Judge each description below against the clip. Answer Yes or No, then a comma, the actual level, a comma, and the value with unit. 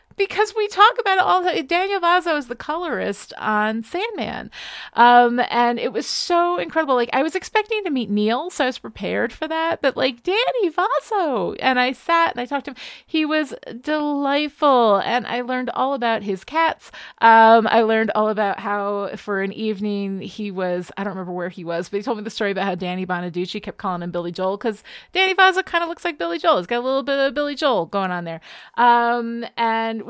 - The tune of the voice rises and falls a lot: Yes, wide, 7.7 semitones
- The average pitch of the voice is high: Yes, high, 240 Hz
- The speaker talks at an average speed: No, fast, 220 wpm